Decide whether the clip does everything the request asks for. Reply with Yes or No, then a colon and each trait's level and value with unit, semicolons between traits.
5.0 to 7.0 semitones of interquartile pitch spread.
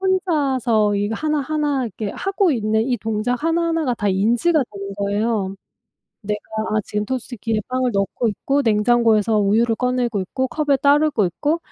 Yes: average, 5.3 semitones